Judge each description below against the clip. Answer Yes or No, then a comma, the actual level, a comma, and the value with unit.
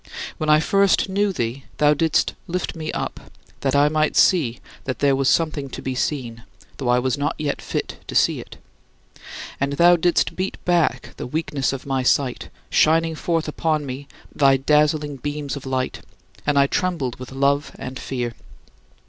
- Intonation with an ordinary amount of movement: Yes, average, 3.0 semitones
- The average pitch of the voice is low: No, medium, 145 Hz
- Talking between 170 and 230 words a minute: Yes, average, 175 wpm